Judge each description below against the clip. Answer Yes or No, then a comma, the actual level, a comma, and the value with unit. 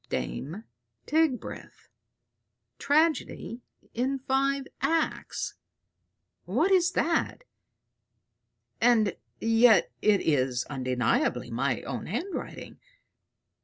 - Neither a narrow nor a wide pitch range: No, wide, 7.4 semitones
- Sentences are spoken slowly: Yes, slow, 75 wpm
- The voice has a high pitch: Yes, high, 245 Hz